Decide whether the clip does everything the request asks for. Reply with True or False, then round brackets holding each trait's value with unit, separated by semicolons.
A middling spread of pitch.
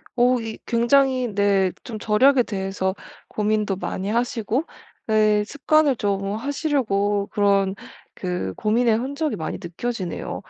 True (3.9 semitones)